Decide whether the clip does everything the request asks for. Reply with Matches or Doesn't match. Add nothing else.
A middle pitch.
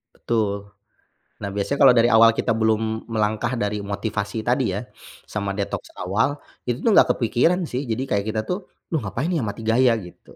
Doesn't match